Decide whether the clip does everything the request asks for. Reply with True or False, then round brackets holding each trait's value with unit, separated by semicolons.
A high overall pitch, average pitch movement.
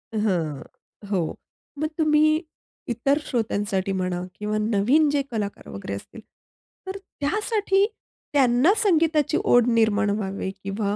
False (225 Hz; 7.1 semitones)